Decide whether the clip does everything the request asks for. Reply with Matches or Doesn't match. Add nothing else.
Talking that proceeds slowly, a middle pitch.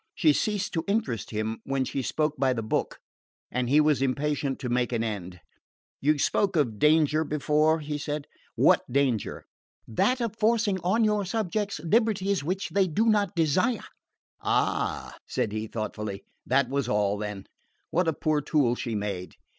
Doesn't match